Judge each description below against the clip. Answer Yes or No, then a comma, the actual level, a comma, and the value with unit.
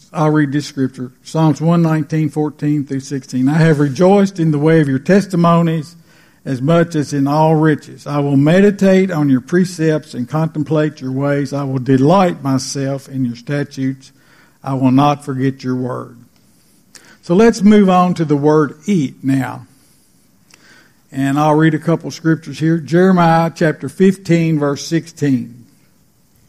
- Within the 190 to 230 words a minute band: No, average, 160 wpm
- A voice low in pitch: No, medium, 150 Hz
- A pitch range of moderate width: Yes, average, 3.3 semitones